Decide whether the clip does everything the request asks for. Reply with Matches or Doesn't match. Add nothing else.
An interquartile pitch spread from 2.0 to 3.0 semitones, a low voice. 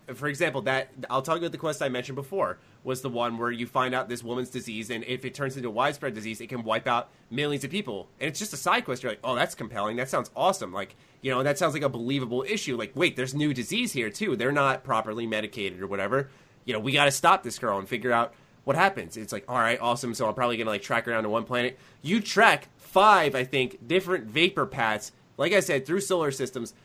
Doesn't match